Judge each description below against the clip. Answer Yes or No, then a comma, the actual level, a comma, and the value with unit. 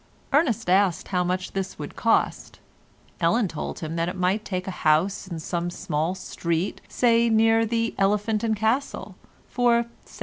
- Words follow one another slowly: No, average, 165 wpm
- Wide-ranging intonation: No, average, 4.3 semitones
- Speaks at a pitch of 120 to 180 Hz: No, high, 195 Hz